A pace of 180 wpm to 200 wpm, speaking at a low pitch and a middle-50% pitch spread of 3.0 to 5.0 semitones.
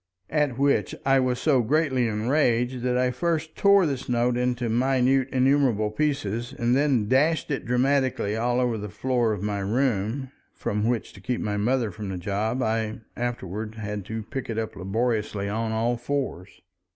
No: average, 170 wpm; low, 120 Hz; average, 3.5 semitones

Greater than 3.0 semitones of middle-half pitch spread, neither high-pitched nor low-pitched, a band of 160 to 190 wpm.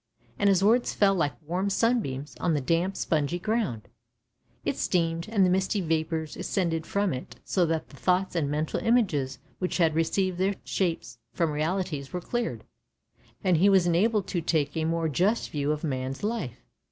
Yes: average, 4.1 semitones; medium, 170 Hz; average, 175 wpm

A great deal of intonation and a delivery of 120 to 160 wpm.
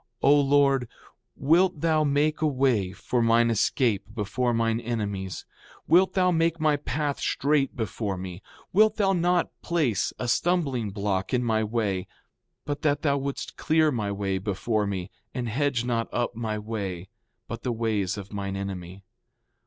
Yes: wide, 6.0 semitones; average, 155 wpm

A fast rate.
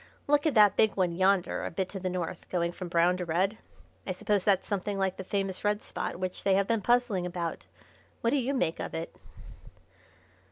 Yes: fast, 210 wpm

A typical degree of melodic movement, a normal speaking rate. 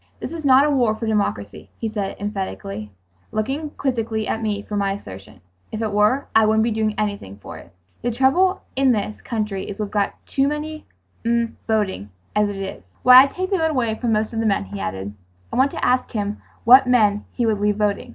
No: average, 3.8 semitones; fast, 220 wpm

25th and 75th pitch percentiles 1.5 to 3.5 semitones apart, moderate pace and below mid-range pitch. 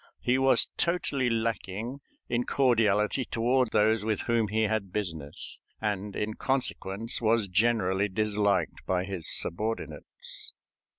No: average, 3.1 semitones; slow, 120 wpm; low, 110 Hz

